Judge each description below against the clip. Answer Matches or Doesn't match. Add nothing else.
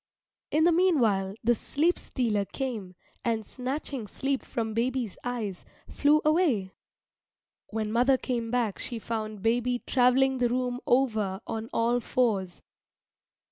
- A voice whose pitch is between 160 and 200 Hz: Doesn't match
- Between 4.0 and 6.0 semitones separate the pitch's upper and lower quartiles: Doesn't match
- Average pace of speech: Doesn't match